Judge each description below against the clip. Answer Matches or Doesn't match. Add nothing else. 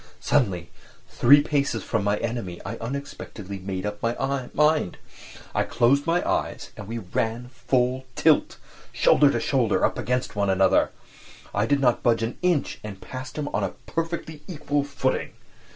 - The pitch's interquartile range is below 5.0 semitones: Doesn't match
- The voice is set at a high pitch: Doesn't match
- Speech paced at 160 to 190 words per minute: Doesn't match